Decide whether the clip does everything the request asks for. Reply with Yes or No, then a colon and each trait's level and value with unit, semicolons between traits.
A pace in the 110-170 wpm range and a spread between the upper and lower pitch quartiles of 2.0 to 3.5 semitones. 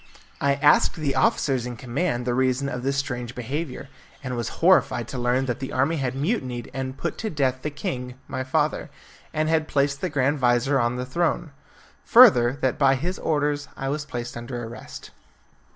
No: average, 185 wpm; average, 2.9 semitones